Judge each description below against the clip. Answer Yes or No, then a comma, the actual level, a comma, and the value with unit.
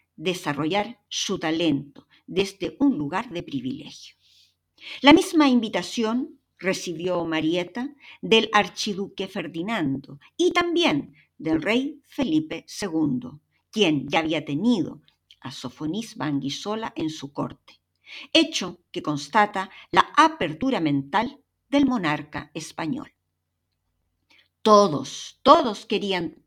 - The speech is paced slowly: Yes, slow, 100 wpm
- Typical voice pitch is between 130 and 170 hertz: No, high, 205 Hz